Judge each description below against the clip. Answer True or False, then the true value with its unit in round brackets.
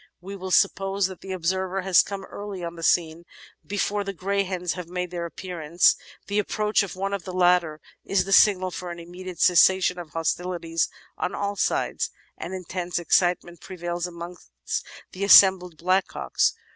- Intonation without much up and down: True (1.9 semitones)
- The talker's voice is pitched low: False (180 Hz)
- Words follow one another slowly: False (170 wpm)